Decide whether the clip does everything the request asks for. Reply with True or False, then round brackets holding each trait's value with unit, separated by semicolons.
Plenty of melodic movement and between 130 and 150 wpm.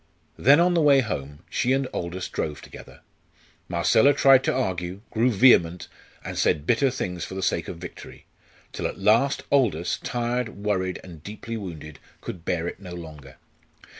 False (6.4 semitones; 165 wpm)